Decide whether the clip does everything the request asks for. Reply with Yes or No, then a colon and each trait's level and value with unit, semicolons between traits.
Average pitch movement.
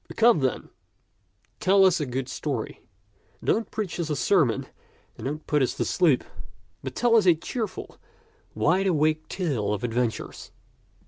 No: wide, 6.4 semitones